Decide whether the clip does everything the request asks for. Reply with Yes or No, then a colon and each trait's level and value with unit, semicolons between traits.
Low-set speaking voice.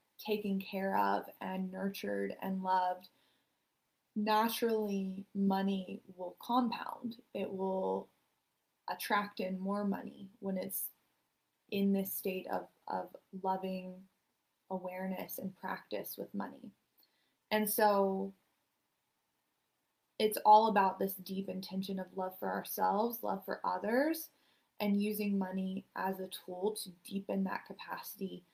No: high, 195 Hz